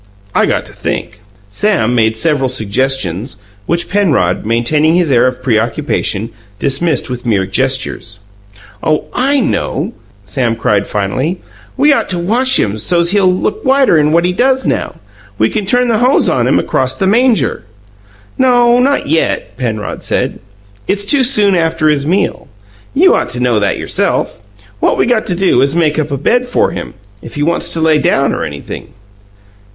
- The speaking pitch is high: No, medium, 155 Hz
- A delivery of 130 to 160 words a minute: No, average, 175 wpm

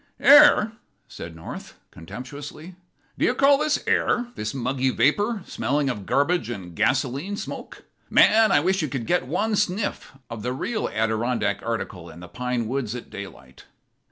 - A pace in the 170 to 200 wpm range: No, average, 155 wpm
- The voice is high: No, low, 135 Hz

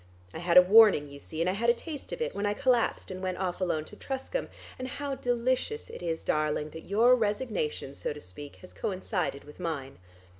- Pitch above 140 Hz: Yes, medium, 185 Hz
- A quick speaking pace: Yes, fast, 220 wpm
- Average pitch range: No, wide, 7.3 semitones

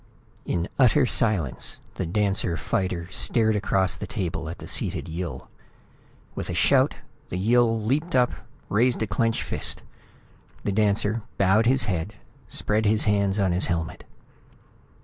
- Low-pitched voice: Yes, low, 105 Hz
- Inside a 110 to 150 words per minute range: Yes, average, 145 wpm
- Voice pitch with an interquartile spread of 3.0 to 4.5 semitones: Yes, average, 3.8 semitones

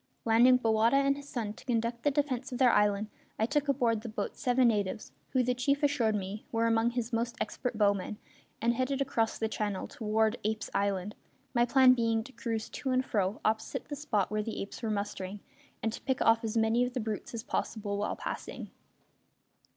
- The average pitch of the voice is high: Yes, high, 230 Hz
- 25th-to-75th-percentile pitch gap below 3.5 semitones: Yes, average, 2.8 semitones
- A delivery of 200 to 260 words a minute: Yes, fast, 205 wpm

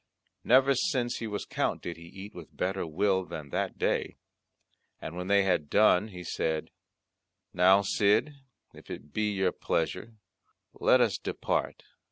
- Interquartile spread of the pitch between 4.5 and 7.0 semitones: No, average, 3.4 semitones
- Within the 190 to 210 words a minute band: No, average, 155 wpm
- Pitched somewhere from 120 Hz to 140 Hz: No, very low, 95 Hz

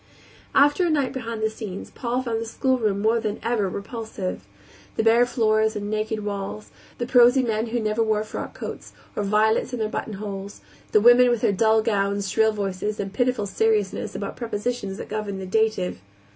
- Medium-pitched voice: No, high, 220 Hz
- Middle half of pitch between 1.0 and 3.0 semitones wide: Yes, narrow, 2.4 semitones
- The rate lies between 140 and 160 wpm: No, average, 185 wpm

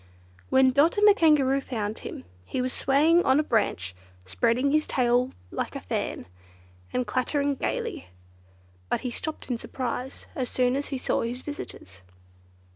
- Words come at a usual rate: Yes, average, 170 wpm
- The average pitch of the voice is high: Yes, very high, 260 Hz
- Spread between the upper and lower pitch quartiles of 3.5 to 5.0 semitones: No, average, 3.1 semitones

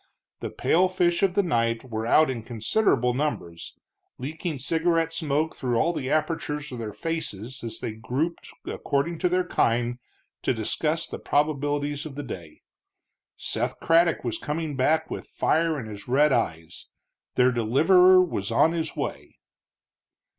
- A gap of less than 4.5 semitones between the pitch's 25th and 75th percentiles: No, wide, 5.5 semitones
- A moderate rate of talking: Yes, average, 155 wpm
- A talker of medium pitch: Yes, medium, 145 Hz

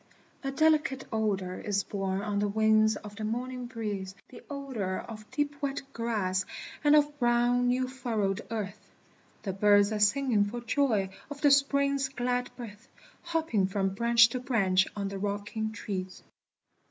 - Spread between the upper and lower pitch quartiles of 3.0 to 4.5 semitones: Yes, average, 4.2 semitones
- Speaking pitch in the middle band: No, high, 220 Hz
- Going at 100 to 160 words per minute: Yes, average, 155 wpm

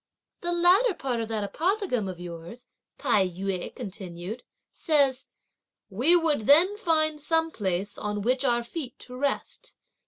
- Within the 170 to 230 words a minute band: No, average, 145 wpm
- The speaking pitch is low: No, very high, 250 Hz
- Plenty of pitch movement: Yes, wide, 8.1 semitones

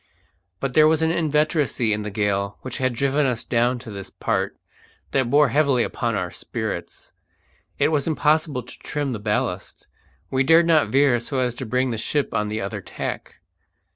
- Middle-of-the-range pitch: No, low, 130 Hz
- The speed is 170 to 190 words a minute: Yes, average, 185 wpm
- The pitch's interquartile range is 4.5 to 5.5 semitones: Yes, average, 5.0 semitones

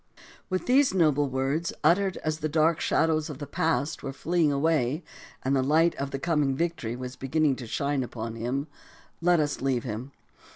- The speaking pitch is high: No, medium, 145 Hz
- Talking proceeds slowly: No, average, 180 wpm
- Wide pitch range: No, average, 3.5 semitones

